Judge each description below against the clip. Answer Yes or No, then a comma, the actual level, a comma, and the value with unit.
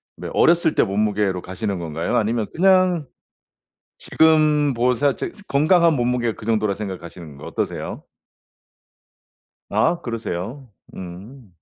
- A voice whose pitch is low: Yes, low, 115 Hz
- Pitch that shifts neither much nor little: No, wide, 7.2 semitones